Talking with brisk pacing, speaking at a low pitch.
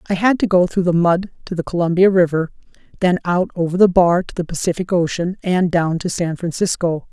No: fast, 210 wpm; medium, 175 Hz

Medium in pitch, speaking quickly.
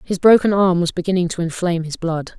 Yes: medium, 175 Hz; fast, 225 wpm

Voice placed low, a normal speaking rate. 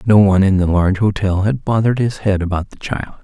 No: low, 100 Hz; fast, 240 wpm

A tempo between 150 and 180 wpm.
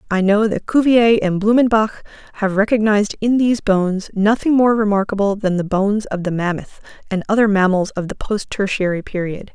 Yes: average, 175 wpm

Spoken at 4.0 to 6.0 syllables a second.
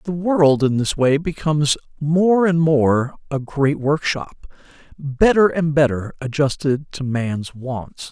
No: 3.7 syllables/s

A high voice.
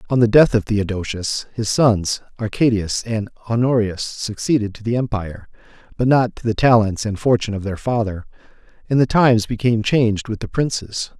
No: low, 110 Hz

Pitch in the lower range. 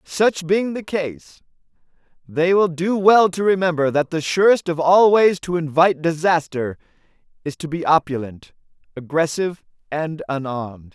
No: medium, 165 Hz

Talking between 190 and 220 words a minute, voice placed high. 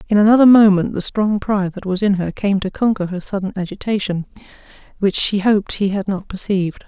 Yes: average, 200 wpm; high, 200 Hz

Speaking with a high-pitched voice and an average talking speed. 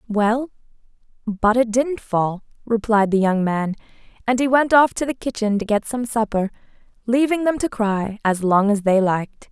Yes: high, 225 Hz; average, 185 wpm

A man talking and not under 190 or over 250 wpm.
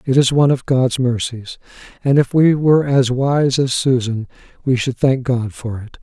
Yes: male; average, 200 wpm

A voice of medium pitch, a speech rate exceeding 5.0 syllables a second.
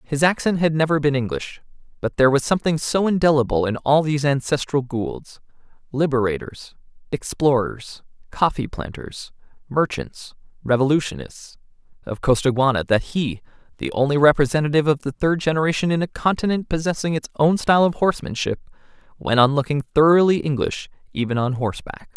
Yes: medium, 145 Hz; 5.6 syllables/s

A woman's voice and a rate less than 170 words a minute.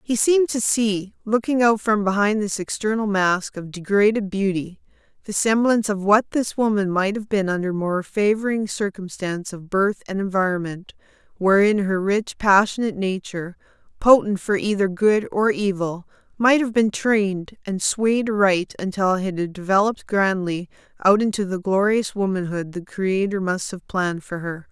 Yes: female; average, 160 wpm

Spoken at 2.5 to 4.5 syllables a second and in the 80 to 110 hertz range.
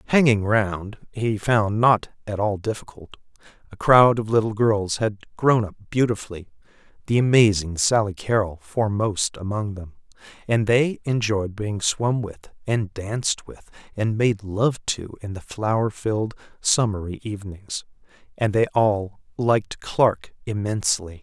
Yes: 4.3 syllables/s; low, 105 Hz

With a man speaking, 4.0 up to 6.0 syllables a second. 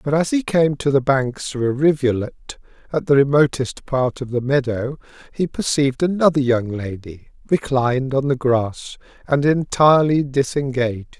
Yes: male; 4.5 syllables/s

